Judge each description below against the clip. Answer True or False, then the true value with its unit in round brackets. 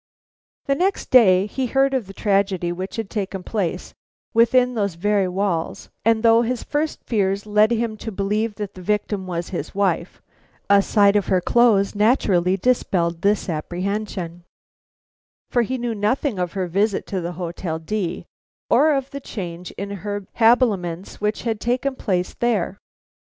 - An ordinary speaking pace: True (160 wpm)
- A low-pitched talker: False (205 Hz)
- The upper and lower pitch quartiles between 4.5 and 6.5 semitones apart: False (3.8 semitones)